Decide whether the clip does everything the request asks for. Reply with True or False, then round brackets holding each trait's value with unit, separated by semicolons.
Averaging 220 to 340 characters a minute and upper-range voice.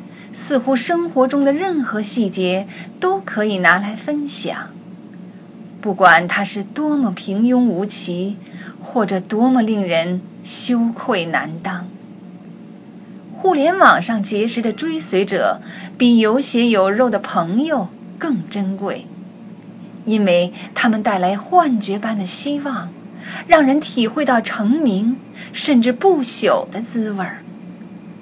False (180 characters per minute; 210 Hz)